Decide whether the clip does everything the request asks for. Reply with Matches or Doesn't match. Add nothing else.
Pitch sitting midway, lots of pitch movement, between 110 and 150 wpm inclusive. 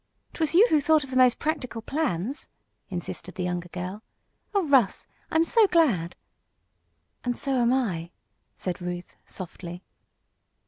Doesn't match